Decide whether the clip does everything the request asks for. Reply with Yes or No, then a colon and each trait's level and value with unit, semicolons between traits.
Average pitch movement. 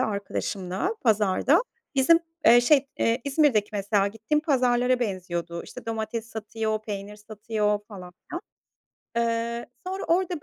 Yes: average, 3.7 semitones